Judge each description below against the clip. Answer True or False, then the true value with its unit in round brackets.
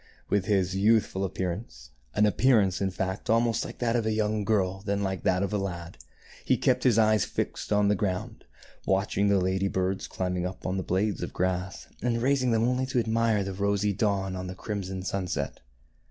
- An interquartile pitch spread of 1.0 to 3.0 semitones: True (2.6 semitones)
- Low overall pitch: True (100 Hz)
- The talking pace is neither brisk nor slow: False (210 wpm)